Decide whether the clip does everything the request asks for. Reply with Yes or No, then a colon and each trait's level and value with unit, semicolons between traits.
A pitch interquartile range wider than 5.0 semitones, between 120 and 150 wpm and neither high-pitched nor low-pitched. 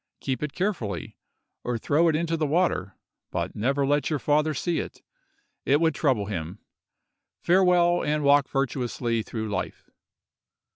Yes: wide, 5.5 semitones; average, 140 wpm; medium, 145 Hz